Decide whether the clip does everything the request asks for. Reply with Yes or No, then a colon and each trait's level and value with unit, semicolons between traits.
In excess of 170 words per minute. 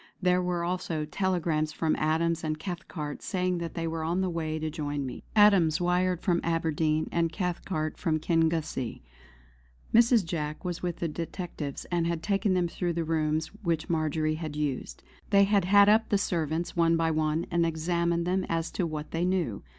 Yes: average, 180 wpm